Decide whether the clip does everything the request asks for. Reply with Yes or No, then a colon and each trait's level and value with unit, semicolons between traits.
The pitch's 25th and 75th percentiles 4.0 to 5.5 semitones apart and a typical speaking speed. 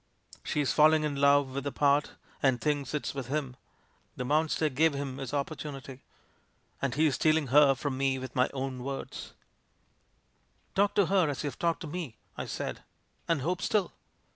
No: narrow, 2.6 semitones; average, 175 wpm